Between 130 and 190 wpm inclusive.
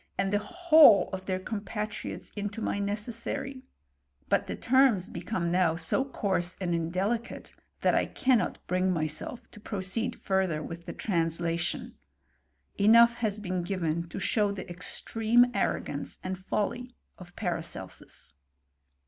Yes: average, 150 wpm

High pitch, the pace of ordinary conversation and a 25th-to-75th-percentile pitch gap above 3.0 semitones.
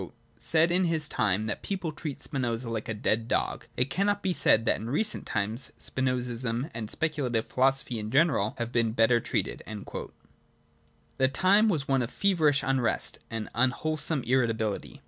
No: low, 130 Hz; average, 175 wpm; average, 5.3 semitones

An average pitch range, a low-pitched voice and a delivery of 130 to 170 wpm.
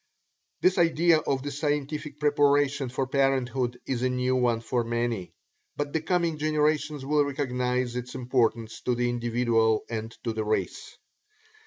Yes: average, 3.4 semitones; low, 130 Hz; average, 150 wpm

